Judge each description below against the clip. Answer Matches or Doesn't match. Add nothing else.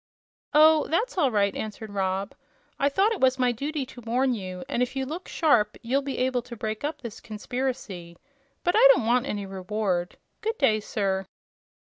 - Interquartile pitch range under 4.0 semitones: Doesn't match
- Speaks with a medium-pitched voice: Doesn't match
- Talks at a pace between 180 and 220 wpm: Matches